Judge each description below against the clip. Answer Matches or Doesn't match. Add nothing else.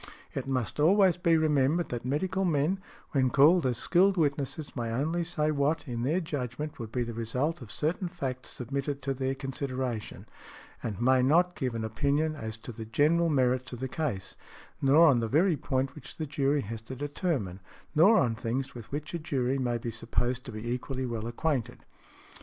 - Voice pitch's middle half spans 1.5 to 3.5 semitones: Doesn't match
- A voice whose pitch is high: Doesn't match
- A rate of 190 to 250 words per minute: Matches